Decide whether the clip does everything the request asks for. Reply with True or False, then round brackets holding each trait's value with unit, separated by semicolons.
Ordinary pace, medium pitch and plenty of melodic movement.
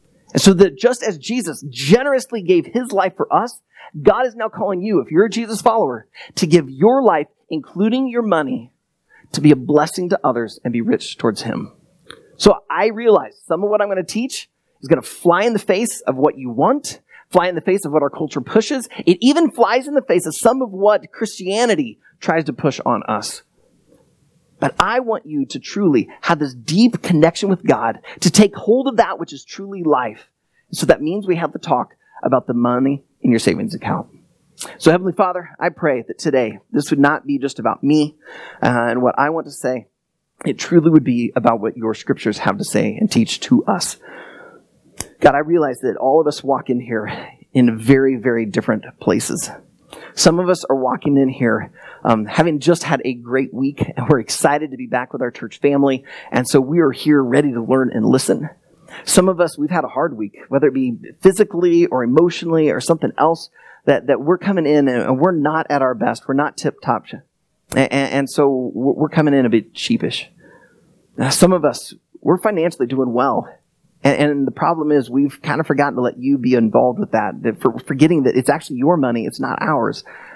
False (215 wpm; 160 Hz; 6.4 semitones)